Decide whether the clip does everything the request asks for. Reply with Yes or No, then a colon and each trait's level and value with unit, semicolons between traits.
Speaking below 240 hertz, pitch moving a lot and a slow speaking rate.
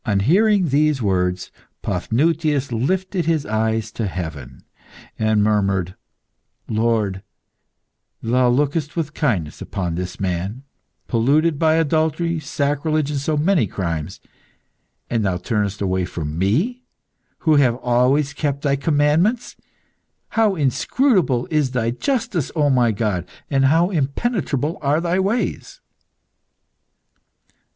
Yes: low, 135 Hz; wide, 7.0 semitones; slow, 115 wpm